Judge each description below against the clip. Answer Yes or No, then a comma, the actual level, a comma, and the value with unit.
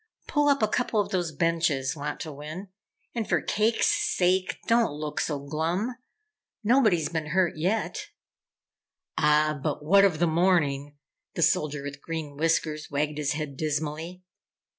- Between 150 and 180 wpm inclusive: No, average, 140 wpm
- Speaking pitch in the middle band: Yes, medium, 160 Hz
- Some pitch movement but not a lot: Yes, average, 3.9 semitones